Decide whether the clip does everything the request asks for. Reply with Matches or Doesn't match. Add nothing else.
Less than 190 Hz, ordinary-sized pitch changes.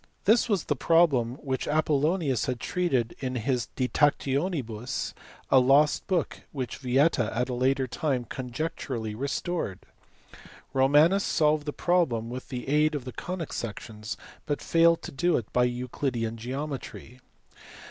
Matches